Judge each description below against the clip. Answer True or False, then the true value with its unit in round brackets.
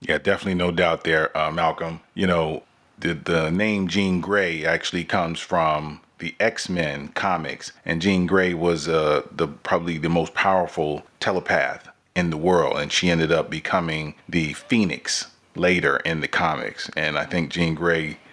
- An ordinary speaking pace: True (165 wpm)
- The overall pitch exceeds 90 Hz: False (85 Hz)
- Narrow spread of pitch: True (2.0 semitones)